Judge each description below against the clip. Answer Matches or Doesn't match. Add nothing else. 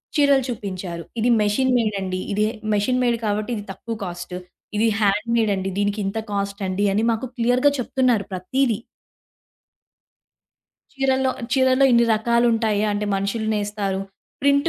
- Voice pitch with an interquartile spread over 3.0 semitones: Matches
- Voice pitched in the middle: Doesn't match